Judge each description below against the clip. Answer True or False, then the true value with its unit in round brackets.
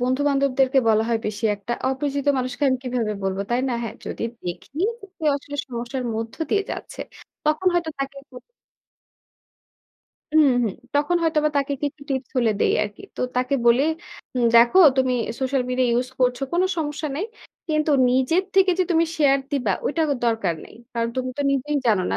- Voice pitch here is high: True (260 Hz)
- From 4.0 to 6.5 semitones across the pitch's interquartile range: False (3.6 semitones)